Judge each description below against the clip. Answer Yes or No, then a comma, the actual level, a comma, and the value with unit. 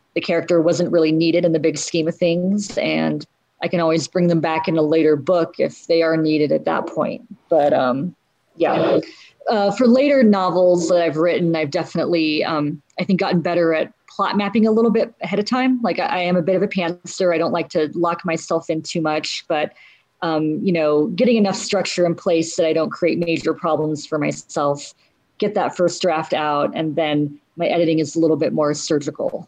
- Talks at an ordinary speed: No, fast, 215 wpm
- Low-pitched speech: No, medium, 170 Hz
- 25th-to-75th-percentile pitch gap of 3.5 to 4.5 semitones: No, average, 2.7 semitones